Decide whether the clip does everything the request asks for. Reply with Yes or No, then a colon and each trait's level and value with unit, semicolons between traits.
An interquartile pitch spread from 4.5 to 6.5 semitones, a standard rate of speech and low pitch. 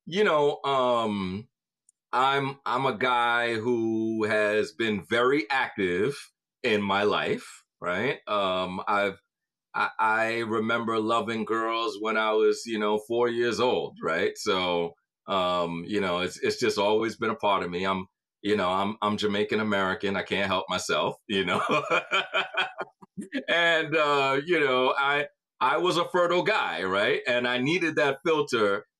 Yes: average, 4.8 semitones; average, 155 wpm; low, 115 Hz